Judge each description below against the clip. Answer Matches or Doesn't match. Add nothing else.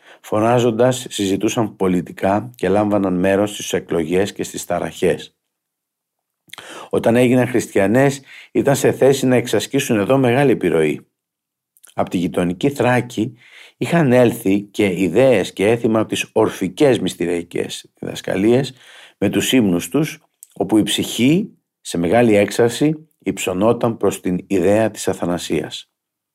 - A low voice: Matches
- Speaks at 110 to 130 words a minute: Matches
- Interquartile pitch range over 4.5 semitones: Doesn't match